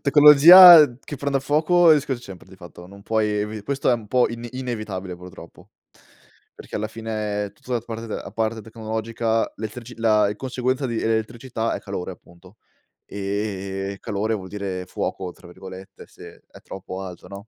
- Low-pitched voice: Yes, low, 110 Hz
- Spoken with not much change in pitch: No, average, 3.7 semitones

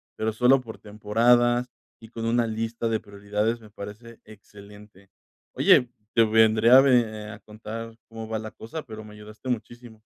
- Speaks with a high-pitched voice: No, low, 110 Hz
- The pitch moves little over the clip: Yes, narrow, 1.8 semitones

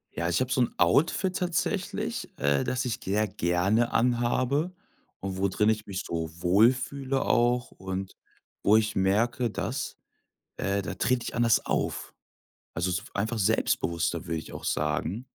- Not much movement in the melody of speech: No, average, 4.9 semitones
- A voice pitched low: Yes, low, 110 Hz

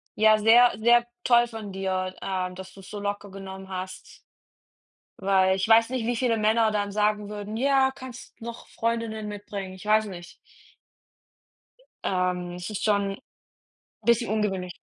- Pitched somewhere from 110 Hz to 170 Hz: No, high, 210 Hz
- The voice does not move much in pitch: No, average, 3.0 semitones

